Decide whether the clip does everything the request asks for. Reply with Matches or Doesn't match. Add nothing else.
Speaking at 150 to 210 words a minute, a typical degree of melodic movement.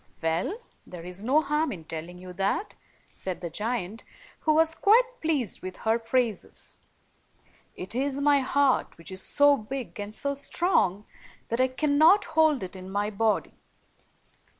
Doesn't match